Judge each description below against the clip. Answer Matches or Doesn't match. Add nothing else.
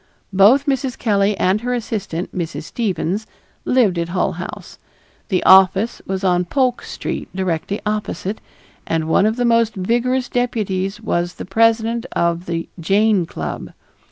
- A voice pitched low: Doesn't match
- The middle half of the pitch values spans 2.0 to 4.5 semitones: Matches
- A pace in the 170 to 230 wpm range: Doesn't match